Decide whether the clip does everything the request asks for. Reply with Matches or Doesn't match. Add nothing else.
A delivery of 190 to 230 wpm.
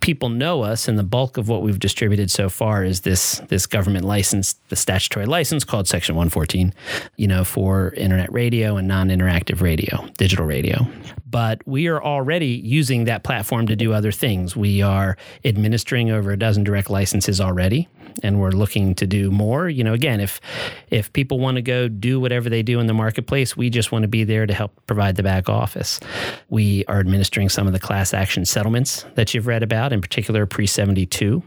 Matches